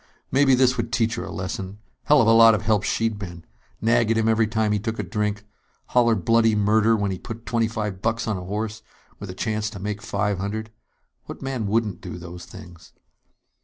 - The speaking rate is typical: No, fast, 215 wpm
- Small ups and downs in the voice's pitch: Yes, narrow, 2.1 semitones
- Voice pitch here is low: Yes, low, 110 Hz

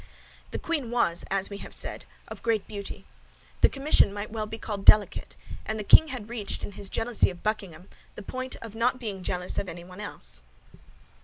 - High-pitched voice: Yes, high, 210 Hz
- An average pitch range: Yes, average, 3.2 semitones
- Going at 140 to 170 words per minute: No, average, 190 wpm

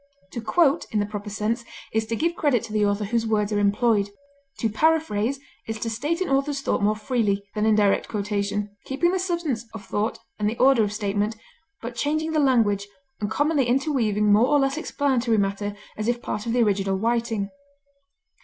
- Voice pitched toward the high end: Yes, high, 225 Hz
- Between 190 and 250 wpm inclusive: Yes, average, 195 wpm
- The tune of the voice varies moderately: Yes, average, 4.7 semitones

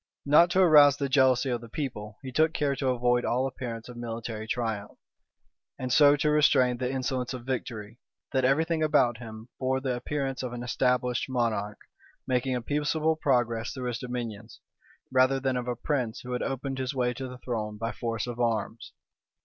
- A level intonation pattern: Yes, narrow, 2.3 semitones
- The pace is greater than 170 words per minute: Yes, average, 190 wpm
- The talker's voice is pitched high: No, low, 125 Hz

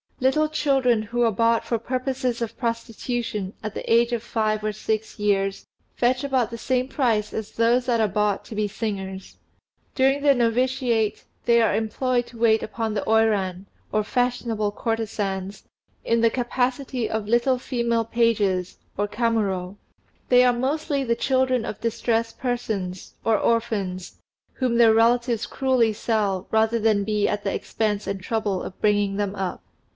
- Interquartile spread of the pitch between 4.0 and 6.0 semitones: No, average, 2.7 semitones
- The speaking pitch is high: Yes, high, 225 Hz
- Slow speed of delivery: No, average, 160 wpm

